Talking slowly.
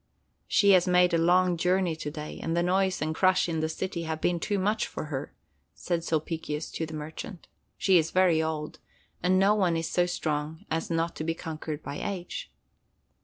No: average, 200 wpm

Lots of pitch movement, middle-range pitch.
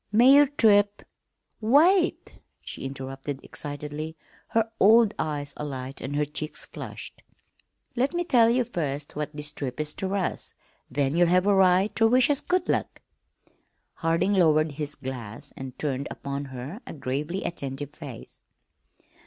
Yes: wide, 7.3 semitones; medium, 155 Hz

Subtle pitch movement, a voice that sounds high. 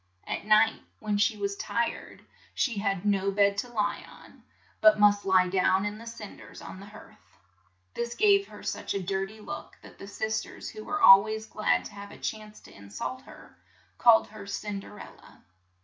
Yes: narrow, 1.7 semitones; high, 210 Hz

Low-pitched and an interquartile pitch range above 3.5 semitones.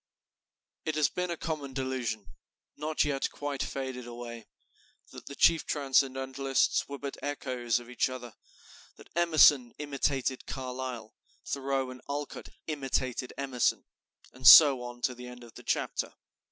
No: low, 130 Hz; narrow, 2.4 semitones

